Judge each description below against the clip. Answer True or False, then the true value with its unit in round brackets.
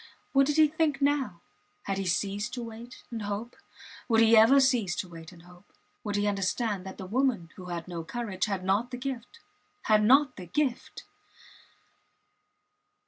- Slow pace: False (175 wpm)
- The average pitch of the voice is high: True (220 Hz)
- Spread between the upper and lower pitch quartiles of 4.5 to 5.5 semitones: True (5.1 semitones)